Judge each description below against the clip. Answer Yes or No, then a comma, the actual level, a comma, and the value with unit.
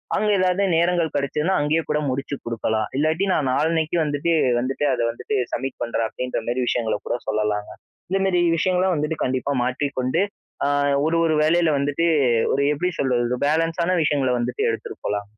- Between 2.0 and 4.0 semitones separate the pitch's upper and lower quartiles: No, average, 4.8 semitones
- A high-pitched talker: No, medium, 145 Hz